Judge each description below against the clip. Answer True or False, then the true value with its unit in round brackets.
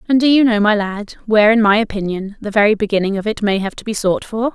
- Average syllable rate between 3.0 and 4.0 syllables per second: False (6.4 syllables/s)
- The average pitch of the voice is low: False (210 Hz)